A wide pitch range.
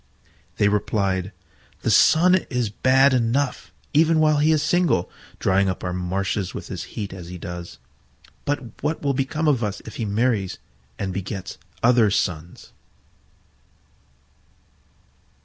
Yes: wide, 6.9 semitones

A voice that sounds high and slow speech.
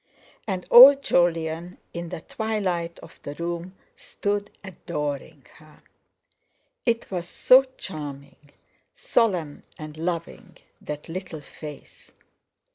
No: medium, 170 Hz; slow, 100 wpm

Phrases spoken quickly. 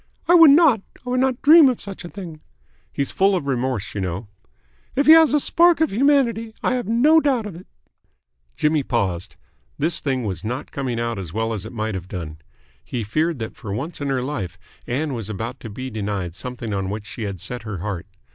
Yes: fast, 220 wpm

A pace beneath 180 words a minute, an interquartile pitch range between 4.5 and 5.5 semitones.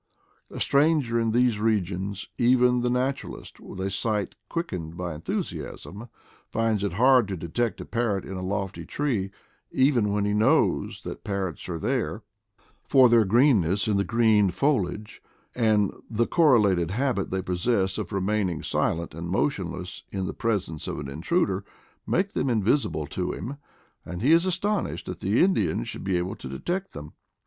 Yes: average, 170 wpm; average, 4.9 semitones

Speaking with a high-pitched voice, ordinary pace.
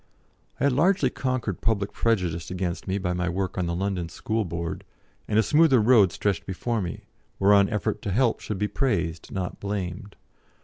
No: low, 100 Hz; average, 180 wpm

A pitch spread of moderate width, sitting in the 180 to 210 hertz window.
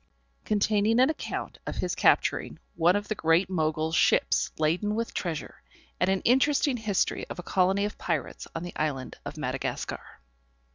Yes: average, 4.7 semitones; high, 190 Hz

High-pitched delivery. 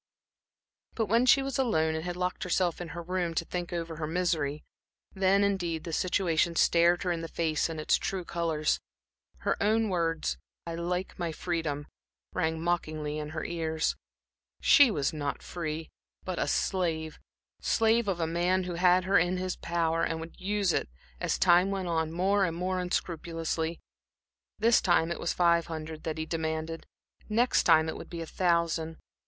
No: medium, 170 Hz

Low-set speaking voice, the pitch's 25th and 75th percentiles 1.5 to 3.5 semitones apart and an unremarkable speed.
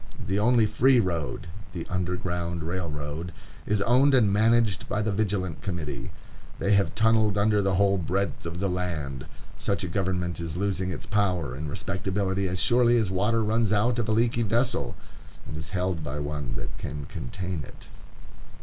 No: very low, 95 Hz; average, 3.9 semitones; average, 170 wpm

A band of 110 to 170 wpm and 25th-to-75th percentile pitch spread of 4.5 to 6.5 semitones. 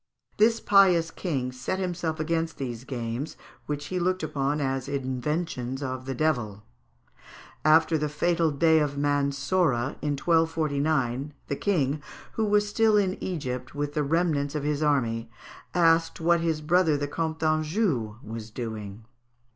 No: average, 145 wpm; average, 3.8 semitones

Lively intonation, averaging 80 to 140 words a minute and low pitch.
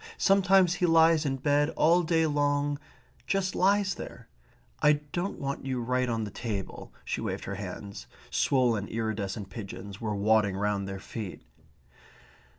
No: wide, 7.8 semitones; average, 150 wpm; low, 130 Hz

